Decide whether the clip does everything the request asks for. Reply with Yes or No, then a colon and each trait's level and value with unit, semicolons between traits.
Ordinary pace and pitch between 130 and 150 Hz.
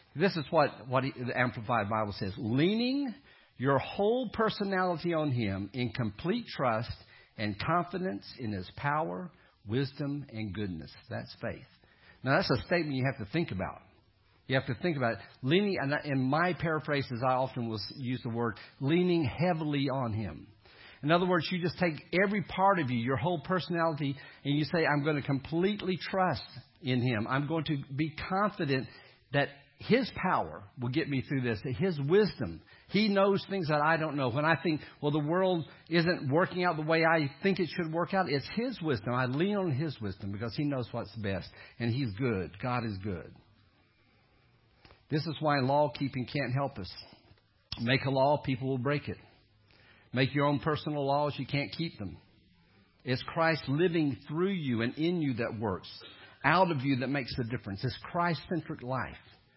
Yes: average, 185 wpm; medium, 140 Hz